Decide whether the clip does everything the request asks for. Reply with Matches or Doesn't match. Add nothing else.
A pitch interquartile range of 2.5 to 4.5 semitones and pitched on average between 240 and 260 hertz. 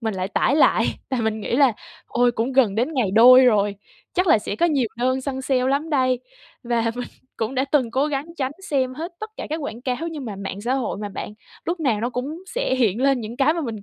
Matches